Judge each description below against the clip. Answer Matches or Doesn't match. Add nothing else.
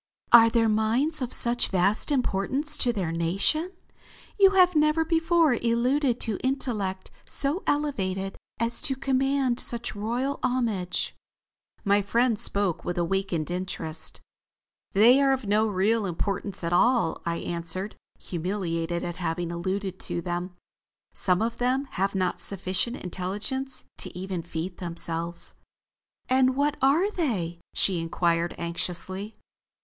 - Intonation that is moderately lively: Doesn't match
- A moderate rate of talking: Doesn't match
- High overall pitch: Matches